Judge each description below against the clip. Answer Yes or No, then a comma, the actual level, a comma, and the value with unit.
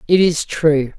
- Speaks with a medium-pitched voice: Yes, medium, 160 Hz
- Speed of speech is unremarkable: Yes, average, 185 wpm